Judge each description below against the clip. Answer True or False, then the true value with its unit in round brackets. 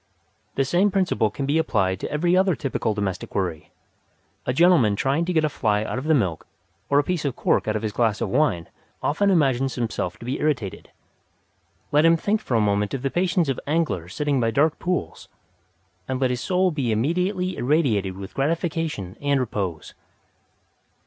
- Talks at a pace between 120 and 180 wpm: False (190 wpm)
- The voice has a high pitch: False (135 Hz)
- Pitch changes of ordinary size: False (7.3 semitones)